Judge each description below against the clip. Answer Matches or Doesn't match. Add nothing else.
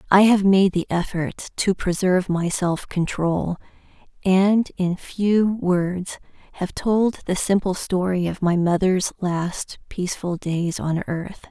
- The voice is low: Doesn't match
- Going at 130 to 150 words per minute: Matches